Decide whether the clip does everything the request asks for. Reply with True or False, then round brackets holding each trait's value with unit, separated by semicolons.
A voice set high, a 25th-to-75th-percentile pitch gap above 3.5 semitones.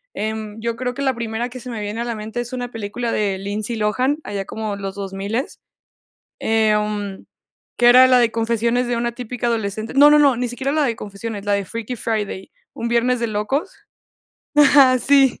False (230 Hz; 2.8 semitones)